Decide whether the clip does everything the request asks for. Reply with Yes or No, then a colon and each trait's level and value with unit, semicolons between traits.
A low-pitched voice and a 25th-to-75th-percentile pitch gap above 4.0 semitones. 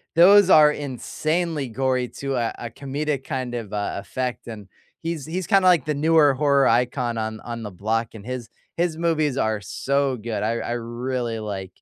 Yes: low, 130 Hz; average, 4.7 semitones